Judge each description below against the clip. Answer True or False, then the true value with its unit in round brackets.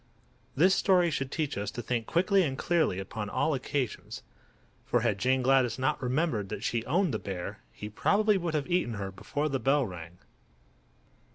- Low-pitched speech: True (130 Hz)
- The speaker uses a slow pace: False (180 wpm)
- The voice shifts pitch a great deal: True (7.2 semitones)